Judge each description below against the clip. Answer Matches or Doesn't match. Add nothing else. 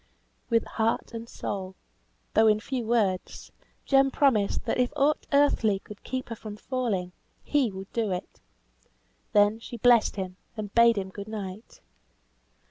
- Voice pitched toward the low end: Doesn't match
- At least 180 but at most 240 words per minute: Doesn't match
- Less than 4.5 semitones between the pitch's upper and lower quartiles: Matches